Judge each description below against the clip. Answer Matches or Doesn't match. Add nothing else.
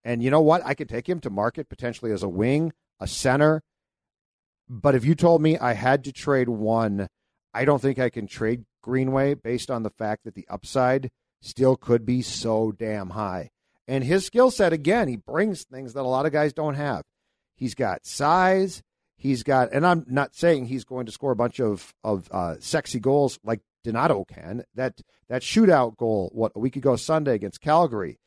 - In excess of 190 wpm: Matches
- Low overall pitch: Matches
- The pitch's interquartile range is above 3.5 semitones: Matches